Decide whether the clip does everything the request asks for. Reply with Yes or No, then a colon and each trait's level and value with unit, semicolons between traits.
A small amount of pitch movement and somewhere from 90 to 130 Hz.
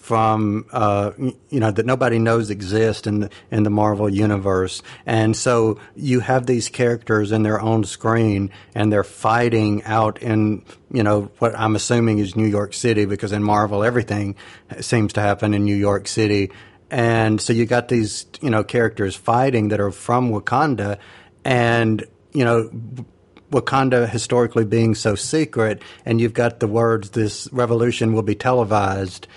Yes: narrow, 2.2 semitones; low, 110 Hz